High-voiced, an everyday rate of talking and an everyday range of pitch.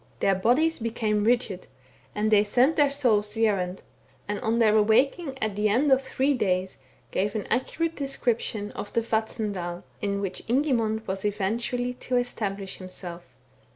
Yes: high, 220 Hz; average, 155 wpm; average, 3.6 semitones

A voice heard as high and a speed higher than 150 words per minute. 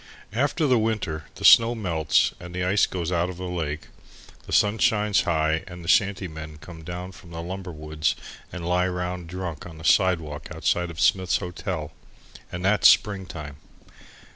No: very low, 90 Hz; average, 180 wpm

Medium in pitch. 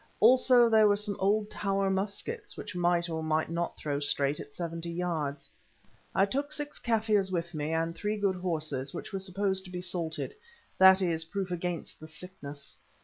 Yes: medium, 180 Hz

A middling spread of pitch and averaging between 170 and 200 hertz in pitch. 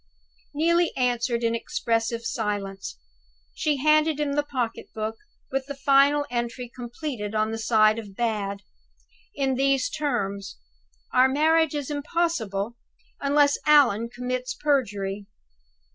No: average, 4.5 semitones; very high, 250 Hz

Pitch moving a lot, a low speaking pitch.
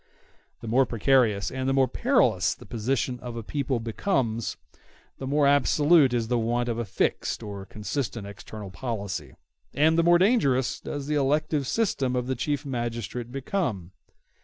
No: average, 3.7 semitones; low, 125 Hz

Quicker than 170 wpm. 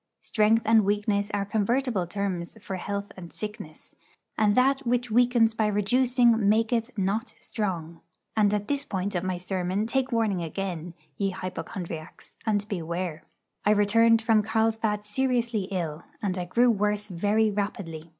No: average, 150 wpm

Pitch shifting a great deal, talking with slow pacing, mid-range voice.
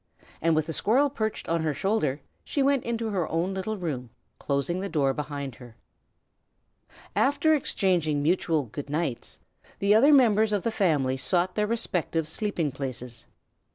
No: wide, 6.8 semitones; average, 155 wpm; medium, 170 Hz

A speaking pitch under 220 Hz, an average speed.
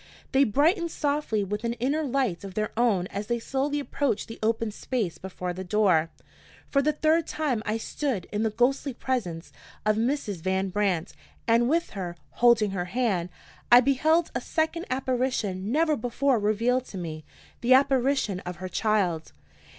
No: high, 230 Hz; average, 165 wpm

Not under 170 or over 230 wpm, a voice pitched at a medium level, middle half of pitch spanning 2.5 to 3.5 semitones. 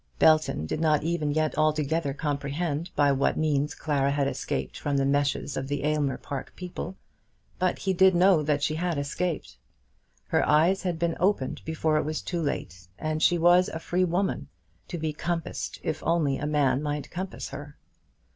Yes: average, 180 wpm; medium, 155 Hz; average, 3.1 semitones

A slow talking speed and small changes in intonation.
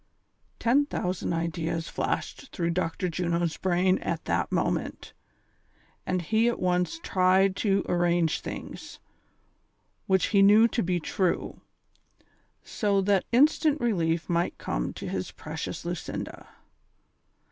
No: slow, 120 wpm; average, 3.0 semitones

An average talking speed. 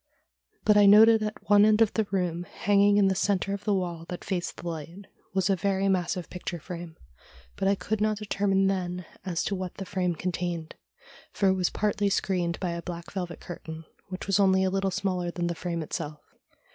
No: fast, 210 wpm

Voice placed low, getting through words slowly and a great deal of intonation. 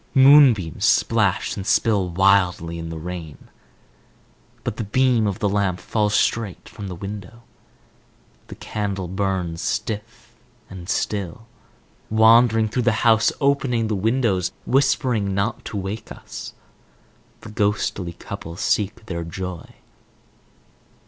No: low, 105 Hz; slow, 120 wpm; average, 3.5 semitones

